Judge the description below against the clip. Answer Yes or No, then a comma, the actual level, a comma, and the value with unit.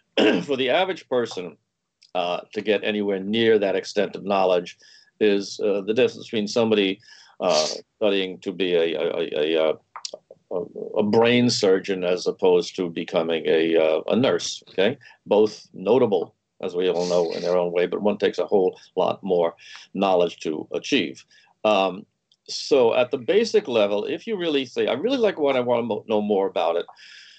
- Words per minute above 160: Yes, average, 175 wpm